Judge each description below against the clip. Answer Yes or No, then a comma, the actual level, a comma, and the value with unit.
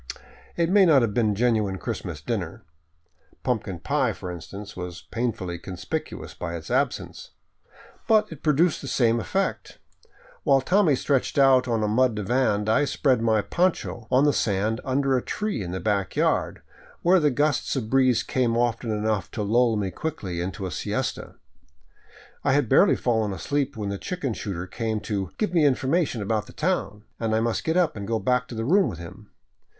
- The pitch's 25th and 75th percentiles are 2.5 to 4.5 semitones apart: No, average, 5.2 semitones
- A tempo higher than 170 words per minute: Yes, average, 185 wpm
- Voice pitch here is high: No, low, 115 Hz